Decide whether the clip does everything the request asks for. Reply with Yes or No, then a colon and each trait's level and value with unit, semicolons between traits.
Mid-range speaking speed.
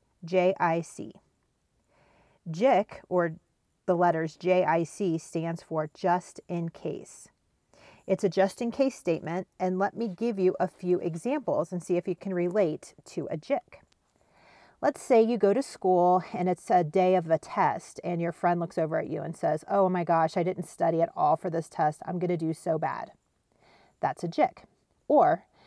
Yes: average, 180 wpm